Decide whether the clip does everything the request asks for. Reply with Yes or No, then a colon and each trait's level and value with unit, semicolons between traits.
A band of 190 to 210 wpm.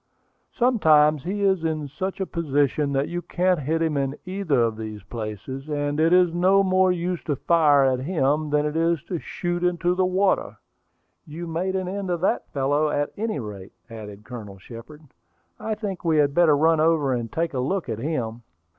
Yes: average, 195 wpm